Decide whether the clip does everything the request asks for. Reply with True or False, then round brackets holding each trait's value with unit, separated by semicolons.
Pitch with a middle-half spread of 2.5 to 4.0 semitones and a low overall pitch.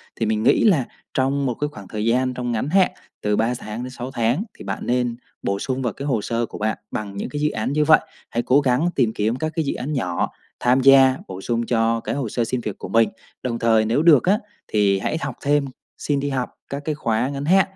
True (3.7 semitones; 125 Hz)